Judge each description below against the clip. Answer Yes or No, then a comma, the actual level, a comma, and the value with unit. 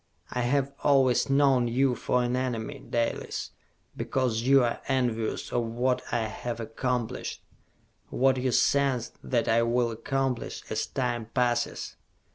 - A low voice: Yes, low, 125 Hz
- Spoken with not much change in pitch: Yes, narrow, 2.0 semitones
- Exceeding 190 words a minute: No, slow, 135 wpm